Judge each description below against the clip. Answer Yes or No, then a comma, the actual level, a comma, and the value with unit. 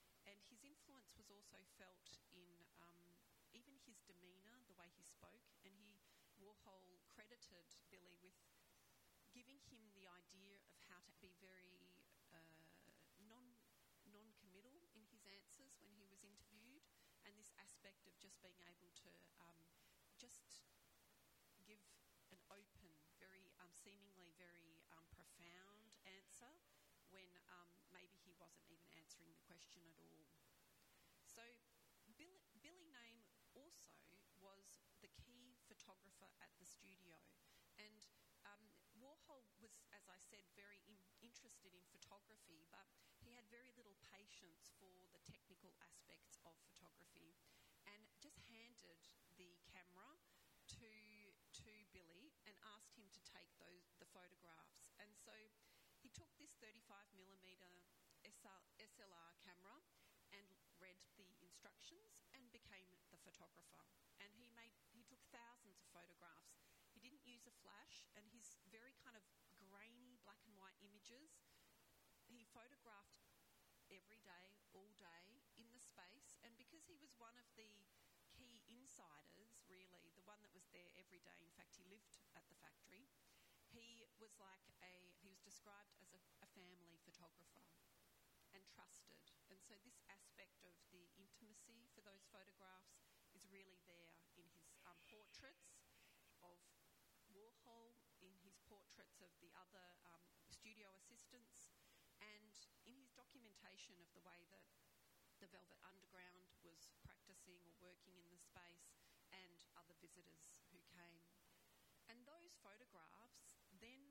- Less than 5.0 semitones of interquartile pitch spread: Yes, average, 3.8 semitones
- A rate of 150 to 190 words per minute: No, average, 140 wpm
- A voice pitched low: No, high, 195 Hz